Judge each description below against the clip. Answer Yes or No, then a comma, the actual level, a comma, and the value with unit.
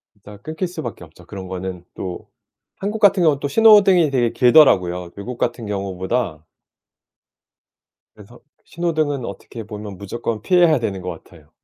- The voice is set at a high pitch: No, low, 115 Hz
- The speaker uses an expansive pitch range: Yes, wide, 8.8 semitones